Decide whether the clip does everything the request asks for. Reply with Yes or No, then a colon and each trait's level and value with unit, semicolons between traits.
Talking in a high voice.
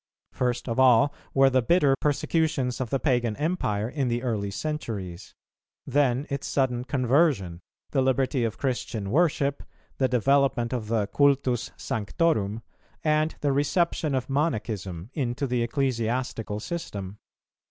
No: low, 130 Hz